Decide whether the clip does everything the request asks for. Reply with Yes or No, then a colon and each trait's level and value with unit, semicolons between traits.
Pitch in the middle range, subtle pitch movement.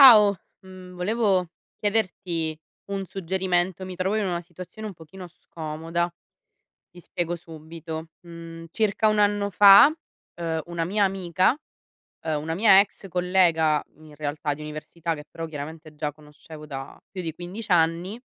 No: medium, 175 Hz; average, 3.1 semitones